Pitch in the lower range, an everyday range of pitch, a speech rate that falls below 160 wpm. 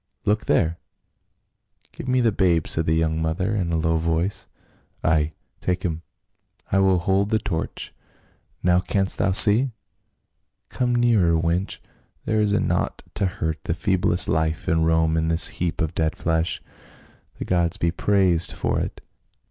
No: very low, 85 Hz; average, 3.3 semitones; average, 165 wpm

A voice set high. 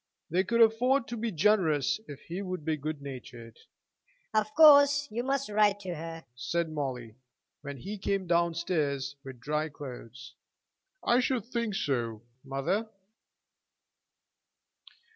No: medium, 170 Hz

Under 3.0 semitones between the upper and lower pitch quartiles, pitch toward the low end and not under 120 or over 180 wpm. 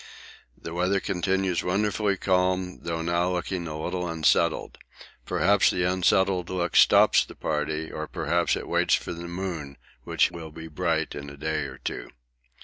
Yes: narrow, 2.6 semitones; very low, 85 Hz; average, 160 wpm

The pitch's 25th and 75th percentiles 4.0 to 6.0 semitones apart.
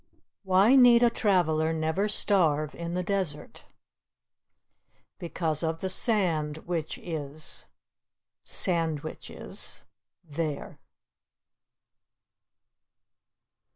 No: average, 3.5 semitones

